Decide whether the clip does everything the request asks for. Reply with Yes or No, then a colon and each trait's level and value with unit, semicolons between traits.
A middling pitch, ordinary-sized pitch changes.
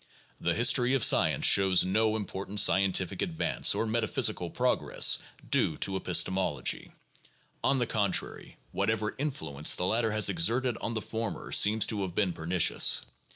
No: low, 105 Hz; average, 3.3 semitones